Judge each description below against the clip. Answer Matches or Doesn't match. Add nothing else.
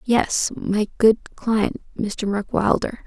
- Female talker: Matches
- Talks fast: Doesn't match